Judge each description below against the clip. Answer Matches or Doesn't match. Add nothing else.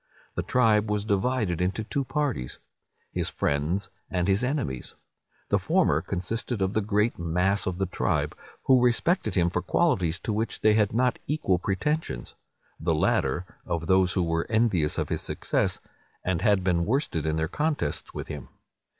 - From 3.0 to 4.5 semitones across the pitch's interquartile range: Doesn't match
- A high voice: Doesn't match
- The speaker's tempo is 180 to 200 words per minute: Doesn't match